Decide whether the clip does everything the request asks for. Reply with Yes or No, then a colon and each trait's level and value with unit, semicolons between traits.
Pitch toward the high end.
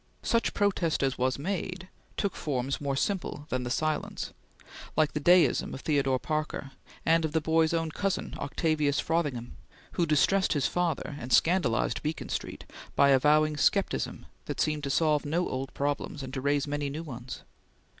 No: medium, 150 Hz